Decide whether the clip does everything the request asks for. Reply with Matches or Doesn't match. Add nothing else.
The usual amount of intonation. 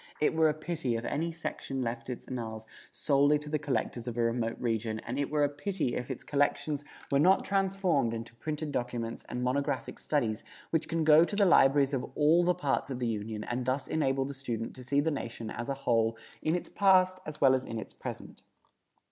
Matches